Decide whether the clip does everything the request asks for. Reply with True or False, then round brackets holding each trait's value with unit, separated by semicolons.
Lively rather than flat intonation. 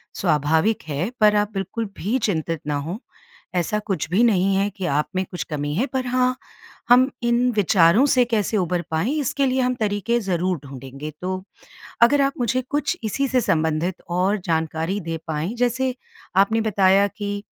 True (6.1 semitones)